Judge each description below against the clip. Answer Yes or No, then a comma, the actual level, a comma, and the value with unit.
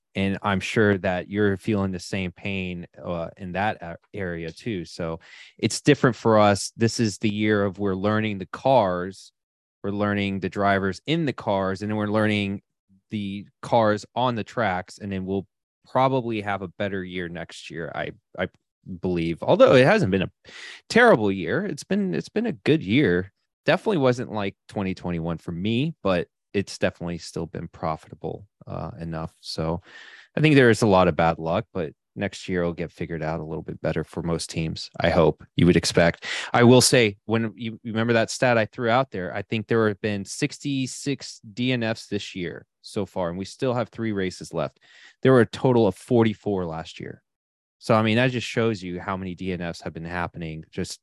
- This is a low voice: Yes, low, 100 Hz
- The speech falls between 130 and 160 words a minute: No, average, 195 wpm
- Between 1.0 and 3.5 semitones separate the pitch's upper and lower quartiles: No, average, 4.0 semitones